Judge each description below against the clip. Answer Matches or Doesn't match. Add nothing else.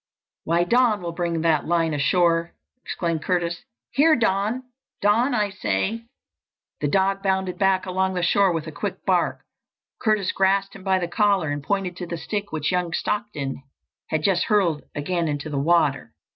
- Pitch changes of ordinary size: Matches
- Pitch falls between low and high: Matches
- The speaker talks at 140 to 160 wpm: Doesn't match